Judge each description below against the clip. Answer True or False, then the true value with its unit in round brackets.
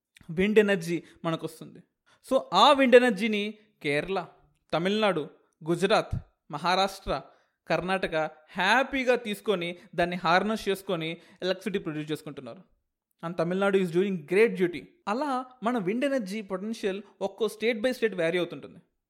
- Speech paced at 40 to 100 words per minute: False (120 wpm)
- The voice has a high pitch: True (195 Hz)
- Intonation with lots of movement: False (4.2 semitones)